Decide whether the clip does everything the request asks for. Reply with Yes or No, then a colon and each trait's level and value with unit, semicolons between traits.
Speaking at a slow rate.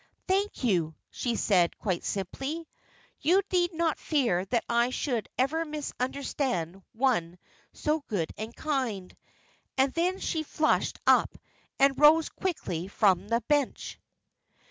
Yes: slow, 125 wpm